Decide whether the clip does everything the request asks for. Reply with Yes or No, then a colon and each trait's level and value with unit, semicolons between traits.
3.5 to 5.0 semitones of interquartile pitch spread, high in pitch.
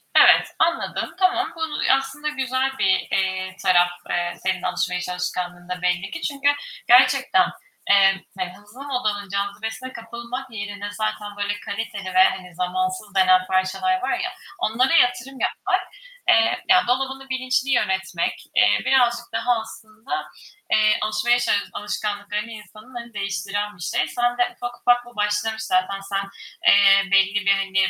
Yes: average, 4.6 semitones; high, 215 Hz